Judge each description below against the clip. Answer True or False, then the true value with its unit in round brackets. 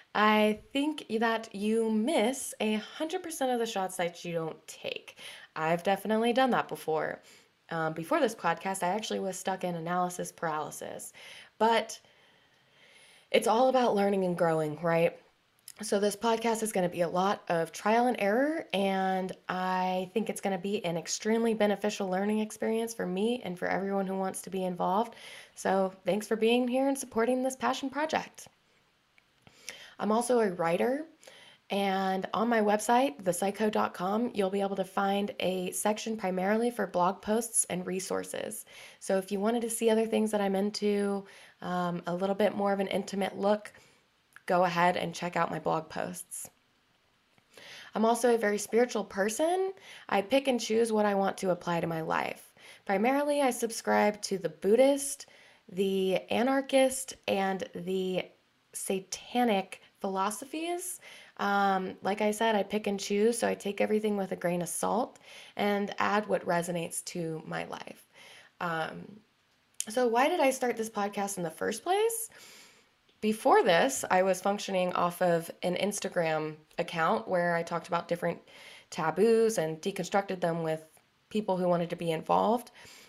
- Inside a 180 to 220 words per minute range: False (165 wpm)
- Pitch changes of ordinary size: True (3.9 semitones)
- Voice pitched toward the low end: False (200 Hz)